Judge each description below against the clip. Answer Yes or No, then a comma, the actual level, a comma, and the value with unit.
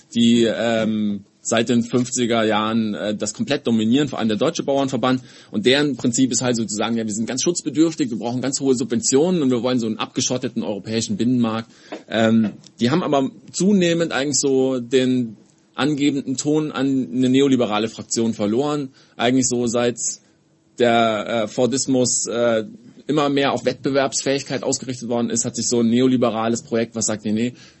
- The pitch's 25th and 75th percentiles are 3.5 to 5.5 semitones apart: No, average, 2.8 semitones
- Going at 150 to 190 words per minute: Yes, average, 170 wpm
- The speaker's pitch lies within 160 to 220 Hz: No, low, 125 Hz